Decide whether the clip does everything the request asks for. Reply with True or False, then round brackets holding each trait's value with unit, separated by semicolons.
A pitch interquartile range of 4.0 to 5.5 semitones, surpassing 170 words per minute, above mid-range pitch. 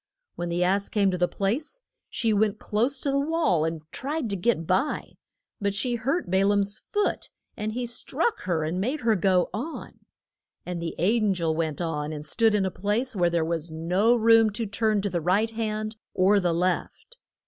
True (4.5 semitones; 200 wpm; 200 Hz)